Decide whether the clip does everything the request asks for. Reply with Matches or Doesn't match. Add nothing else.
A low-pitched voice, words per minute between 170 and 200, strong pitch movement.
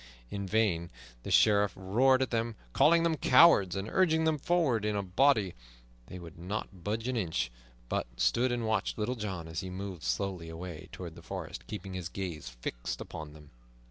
Matches